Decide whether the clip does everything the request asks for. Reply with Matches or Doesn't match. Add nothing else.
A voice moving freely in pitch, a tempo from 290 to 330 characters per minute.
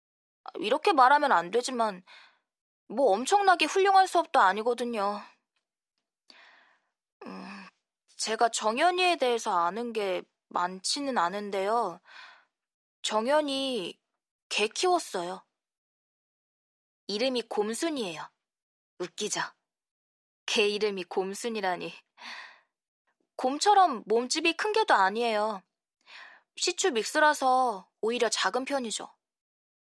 Doesn't match